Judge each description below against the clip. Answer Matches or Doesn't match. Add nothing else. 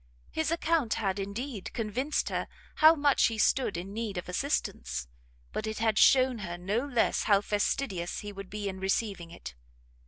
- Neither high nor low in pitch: Doesn't match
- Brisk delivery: Doesn't match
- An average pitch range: Matches